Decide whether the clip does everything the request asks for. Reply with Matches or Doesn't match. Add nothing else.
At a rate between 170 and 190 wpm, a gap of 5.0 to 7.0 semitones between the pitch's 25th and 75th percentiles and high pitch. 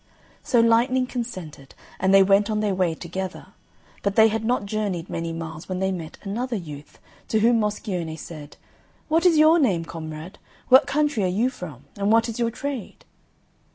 Matches